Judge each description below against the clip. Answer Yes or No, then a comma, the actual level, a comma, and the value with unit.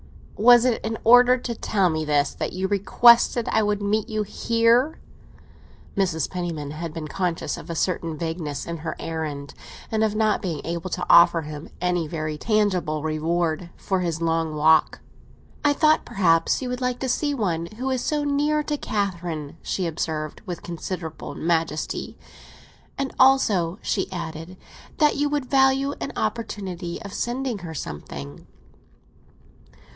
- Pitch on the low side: No, medium, 180 Hz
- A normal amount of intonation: No, wide, 6.4 semitones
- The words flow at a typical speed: Yes, average, 155 wpm